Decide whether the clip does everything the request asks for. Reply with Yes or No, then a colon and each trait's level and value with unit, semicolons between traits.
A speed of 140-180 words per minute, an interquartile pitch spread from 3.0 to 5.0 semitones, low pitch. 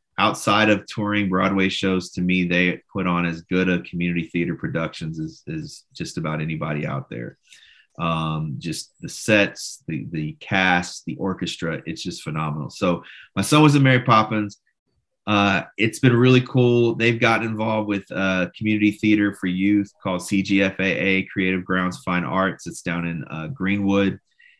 Yes: average, 165 wpm; average, 3.5 semitones; very low, 95 Hz